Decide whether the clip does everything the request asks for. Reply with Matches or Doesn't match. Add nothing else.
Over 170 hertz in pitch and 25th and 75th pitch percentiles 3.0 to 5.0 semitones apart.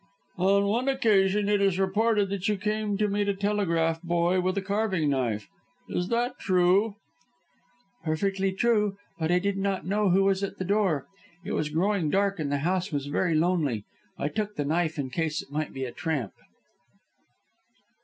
Matches